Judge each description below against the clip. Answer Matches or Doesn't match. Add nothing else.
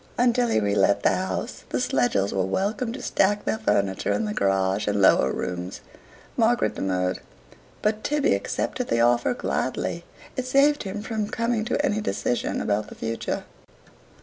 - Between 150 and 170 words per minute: Matches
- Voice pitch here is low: Matches